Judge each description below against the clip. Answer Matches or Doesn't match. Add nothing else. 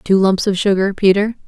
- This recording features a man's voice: Doesn't match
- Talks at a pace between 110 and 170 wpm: Doesn't match